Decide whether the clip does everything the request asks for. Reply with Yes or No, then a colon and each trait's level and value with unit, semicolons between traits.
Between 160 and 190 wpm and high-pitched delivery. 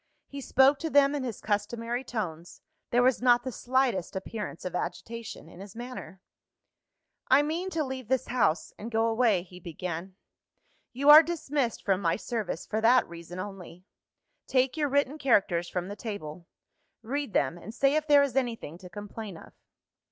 Yes: average, 175 wpm; high, 230 Hz